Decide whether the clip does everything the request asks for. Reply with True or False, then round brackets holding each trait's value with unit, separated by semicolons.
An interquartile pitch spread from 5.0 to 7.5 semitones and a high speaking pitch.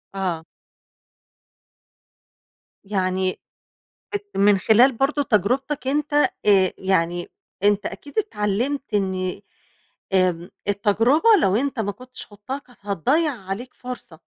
True (5.6 semitones; 205 Hz)